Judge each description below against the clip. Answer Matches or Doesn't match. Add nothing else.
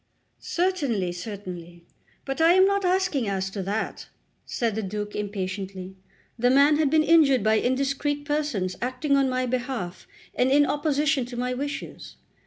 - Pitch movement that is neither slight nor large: Doesn't match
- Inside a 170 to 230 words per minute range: Doesn't match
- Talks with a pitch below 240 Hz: Doesn't match